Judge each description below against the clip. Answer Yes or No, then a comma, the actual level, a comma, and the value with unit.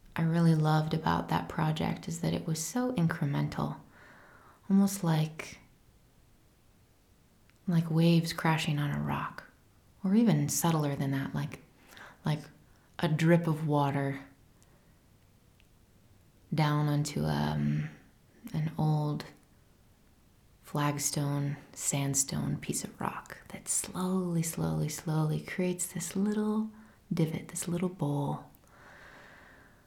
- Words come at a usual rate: No, slow, 105 wpm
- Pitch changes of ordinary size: Yes, average, 3.7 semitones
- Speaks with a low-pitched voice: No, medium, 155 Hz